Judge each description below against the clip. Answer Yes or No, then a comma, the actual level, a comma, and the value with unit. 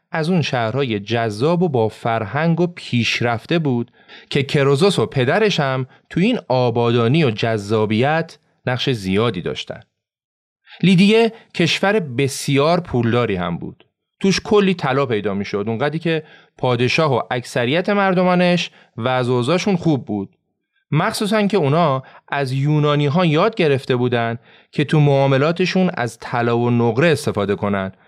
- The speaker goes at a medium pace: Yes, average, 135 wpm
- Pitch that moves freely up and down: Yes, wide, 6.5 semitones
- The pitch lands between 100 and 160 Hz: Yes, medium, 140 Hz